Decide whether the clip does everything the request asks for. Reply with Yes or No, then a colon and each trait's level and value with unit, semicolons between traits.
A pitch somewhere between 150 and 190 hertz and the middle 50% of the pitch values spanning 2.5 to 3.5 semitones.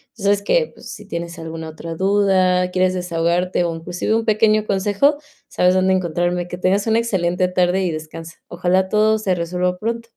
Yes: medium, 185 Hz; average, 2.8 semitones